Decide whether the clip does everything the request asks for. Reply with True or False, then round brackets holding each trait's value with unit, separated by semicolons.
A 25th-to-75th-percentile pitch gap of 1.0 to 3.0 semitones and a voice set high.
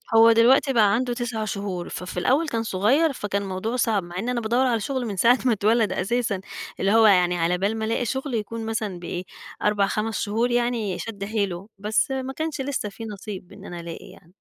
False (3.5 semitones; 220 Hz)